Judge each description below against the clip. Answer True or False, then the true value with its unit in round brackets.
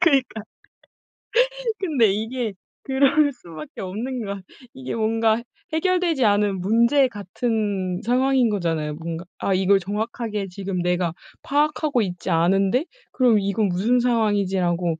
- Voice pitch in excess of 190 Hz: True (210 Hz)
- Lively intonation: False (5.0 semitones)